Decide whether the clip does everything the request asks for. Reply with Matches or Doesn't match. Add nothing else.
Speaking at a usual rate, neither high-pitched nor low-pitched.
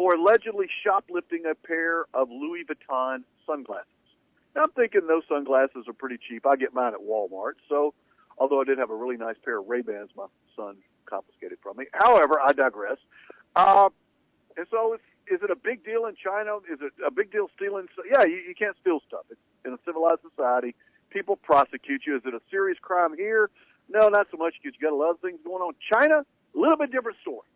Doesn't match